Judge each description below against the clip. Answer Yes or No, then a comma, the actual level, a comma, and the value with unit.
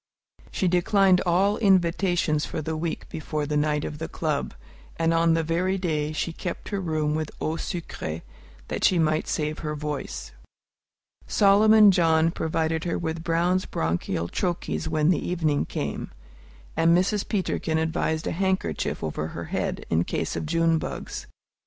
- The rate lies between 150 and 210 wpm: Yes, average, 160 wpm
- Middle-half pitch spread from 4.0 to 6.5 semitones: No, average, 2.7 semitones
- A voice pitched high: No, medium, 165 Hz